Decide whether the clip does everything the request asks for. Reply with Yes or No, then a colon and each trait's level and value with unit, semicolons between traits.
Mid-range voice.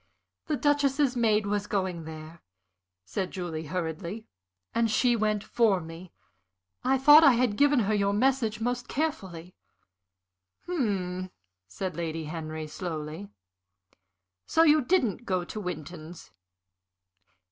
No: high, 200 Hz